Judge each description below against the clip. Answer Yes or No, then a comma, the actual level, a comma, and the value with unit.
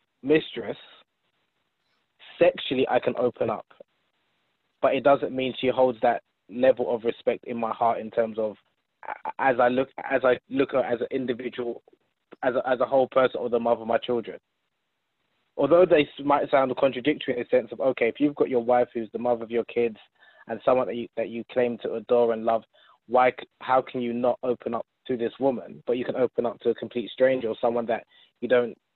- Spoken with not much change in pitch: Yes, narrow, 2.0 semitones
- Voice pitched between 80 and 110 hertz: No, low, 125 Hz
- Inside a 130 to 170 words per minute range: No, fast, 205 wpm